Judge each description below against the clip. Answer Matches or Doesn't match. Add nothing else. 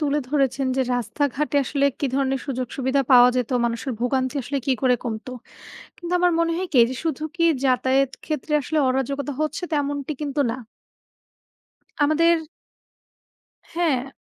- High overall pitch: Matches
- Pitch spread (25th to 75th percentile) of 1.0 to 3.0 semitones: Matches